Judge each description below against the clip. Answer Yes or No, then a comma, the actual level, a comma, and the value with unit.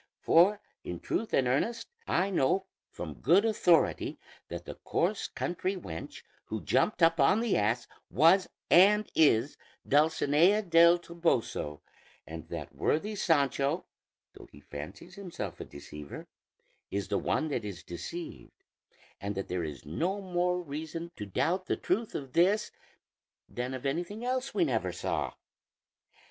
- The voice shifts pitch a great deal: Yes, wide, 7.8 semitones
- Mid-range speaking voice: Yes, medium, 165 Hz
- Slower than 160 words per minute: Yes, average, 145 wpm